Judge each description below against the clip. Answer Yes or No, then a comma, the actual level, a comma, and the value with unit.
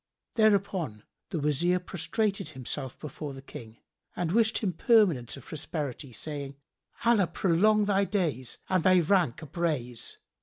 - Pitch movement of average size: No, wide, 6.2 semitones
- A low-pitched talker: No, medium, 170 Hz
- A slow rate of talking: Yes, slow, 130 wpm